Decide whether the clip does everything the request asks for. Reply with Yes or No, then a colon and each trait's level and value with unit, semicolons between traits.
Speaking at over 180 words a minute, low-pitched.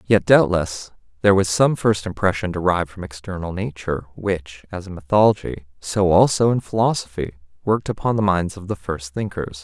No: average, 170 wpm; very low, 95 Hz